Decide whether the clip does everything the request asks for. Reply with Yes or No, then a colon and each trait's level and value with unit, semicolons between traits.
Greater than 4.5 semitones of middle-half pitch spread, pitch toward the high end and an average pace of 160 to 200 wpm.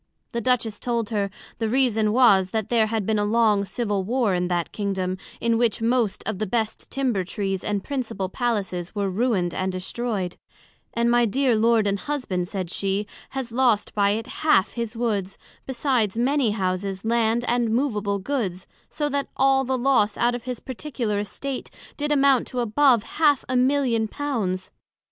No: average, 3.9 semitones; high, 225 Hz; average, 175 wpm